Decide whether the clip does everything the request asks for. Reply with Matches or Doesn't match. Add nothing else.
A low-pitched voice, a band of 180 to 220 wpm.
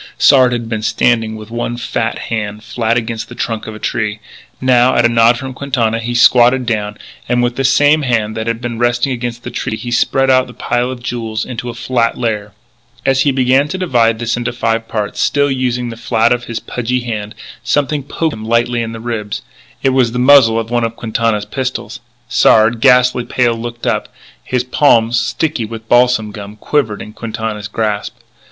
Matches